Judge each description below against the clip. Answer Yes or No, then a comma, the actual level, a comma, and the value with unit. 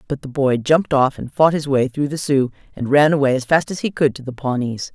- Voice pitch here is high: No, medium, 140 Hz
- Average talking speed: No, fast, 280 wpm